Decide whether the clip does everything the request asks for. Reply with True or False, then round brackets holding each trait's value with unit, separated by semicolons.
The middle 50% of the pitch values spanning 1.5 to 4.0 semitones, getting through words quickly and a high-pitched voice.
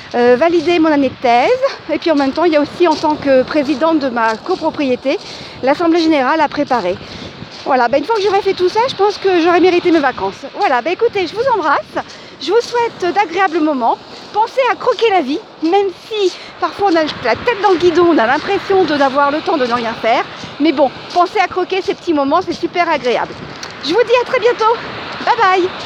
False (5.2 semitones; 225 wpm; 345 Hz)